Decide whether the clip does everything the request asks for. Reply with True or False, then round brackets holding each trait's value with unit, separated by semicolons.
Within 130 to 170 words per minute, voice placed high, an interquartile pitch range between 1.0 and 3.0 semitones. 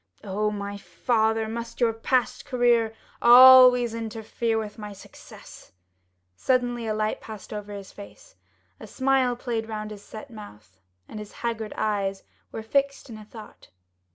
True (145 wpm; 220 Hz; 2.4 semitones)